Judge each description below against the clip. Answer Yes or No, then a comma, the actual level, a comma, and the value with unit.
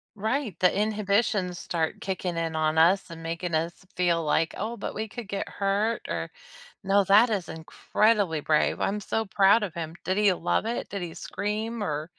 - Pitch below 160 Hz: No, high, 195 Hz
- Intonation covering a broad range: No, average, 4.0 semitones